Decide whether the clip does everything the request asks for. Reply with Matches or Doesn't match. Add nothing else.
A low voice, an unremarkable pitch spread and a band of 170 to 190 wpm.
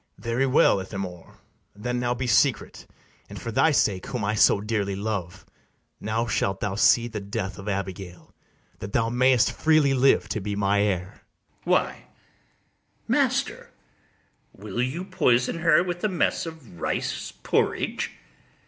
Doesn't match